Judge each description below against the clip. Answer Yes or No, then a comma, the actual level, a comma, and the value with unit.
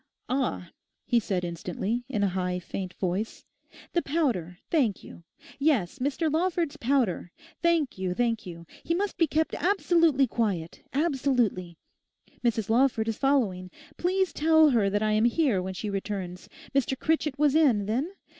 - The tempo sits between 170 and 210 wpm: No, average, 150 wpm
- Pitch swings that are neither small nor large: No, wide, 7.8 semitones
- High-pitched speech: Yes, high, 240 Hz